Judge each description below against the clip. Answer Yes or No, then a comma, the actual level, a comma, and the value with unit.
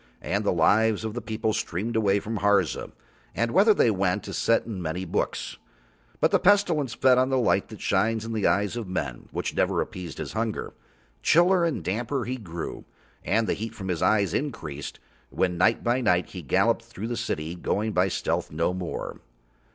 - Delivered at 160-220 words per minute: Yes, average, 195 wpm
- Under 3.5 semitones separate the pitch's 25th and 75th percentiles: No, average, 4.3 semitones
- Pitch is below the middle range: Yes, low, 110 Hz